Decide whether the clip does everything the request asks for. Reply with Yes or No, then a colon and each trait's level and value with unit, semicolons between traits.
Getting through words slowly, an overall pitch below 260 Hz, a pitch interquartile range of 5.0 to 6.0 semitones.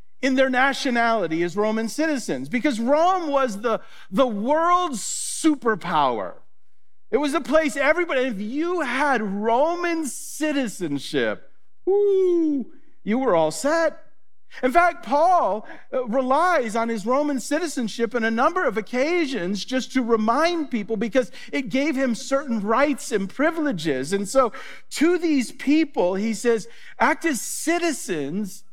No: slow, 130 wpm; very high, 265 Hz; wide, 5.6 semitones